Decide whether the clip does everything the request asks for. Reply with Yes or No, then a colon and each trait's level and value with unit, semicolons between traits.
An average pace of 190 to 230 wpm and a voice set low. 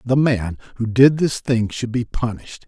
Yes: average, 200 wpm; low, 120 Hz